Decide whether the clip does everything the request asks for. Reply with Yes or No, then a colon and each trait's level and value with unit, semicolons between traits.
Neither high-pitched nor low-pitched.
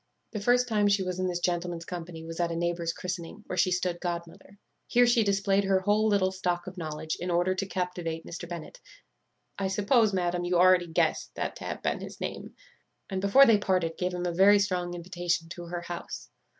Yes: medium, 180 Hz